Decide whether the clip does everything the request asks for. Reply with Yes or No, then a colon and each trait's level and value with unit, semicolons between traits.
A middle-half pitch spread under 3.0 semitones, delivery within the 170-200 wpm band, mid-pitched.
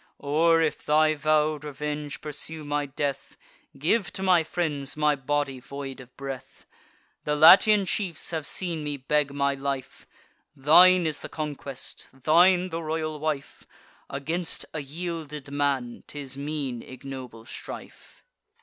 No: narrow, 2.5 semitones; slow, 135 wpm; medium, 150 Hz